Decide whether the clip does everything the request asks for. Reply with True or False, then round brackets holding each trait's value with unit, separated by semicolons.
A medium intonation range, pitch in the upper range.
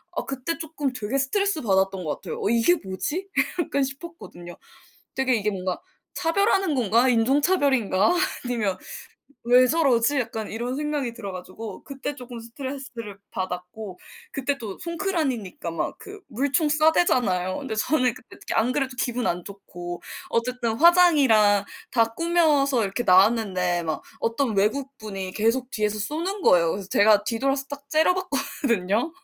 False (5.8 semitones; 245 Hz)